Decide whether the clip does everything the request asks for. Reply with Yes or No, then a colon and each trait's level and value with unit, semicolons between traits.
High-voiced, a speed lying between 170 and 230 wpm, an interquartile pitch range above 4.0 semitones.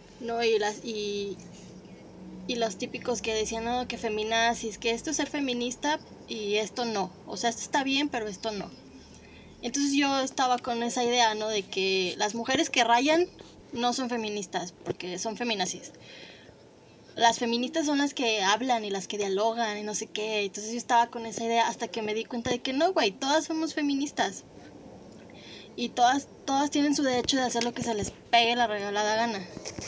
No: high, 230 Hz; fast, 190 wpm; average, 3.0 semitones